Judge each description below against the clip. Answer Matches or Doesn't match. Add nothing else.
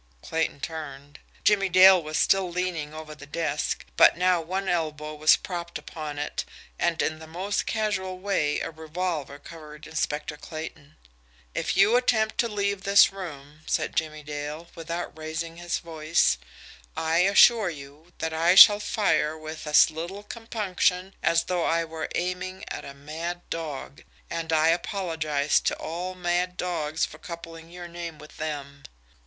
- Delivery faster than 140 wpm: Matches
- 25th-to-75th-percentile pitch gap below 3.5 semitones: Matches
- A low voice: Doesn't match